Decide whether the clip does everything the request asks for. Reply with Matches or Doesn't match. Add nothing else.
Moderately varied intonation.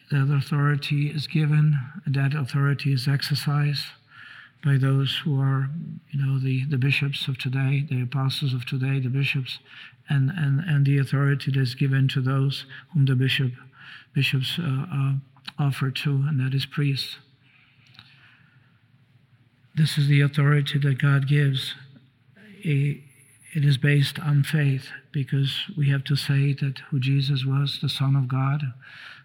Doesn't match